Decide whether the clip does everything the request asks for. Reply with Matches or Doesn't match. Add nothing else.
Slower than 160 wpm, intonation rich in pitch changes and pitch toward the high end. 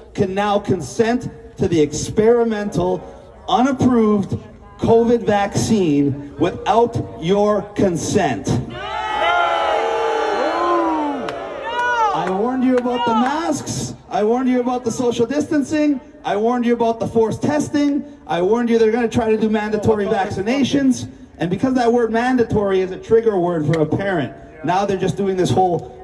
Doesn't match